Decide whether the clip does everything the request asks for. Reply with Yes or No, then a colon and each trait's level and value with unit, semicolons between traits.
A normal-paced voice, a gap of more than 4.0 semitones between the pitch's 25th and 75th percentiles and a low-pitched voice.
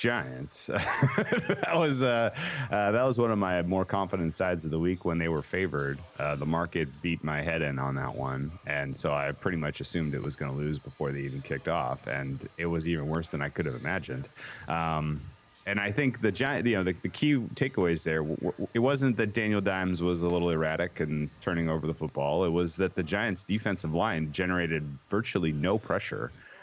No: fast, 215 wpm; average, 4.7 semitones; very low, 85 Hz